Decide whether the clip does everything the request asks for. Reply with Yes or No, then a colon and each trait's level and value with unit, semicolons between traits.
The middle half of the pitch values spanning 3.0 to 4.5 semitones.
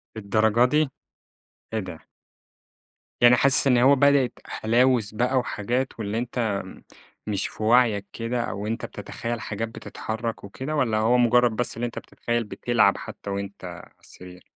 No: narrow, 2.6 semitones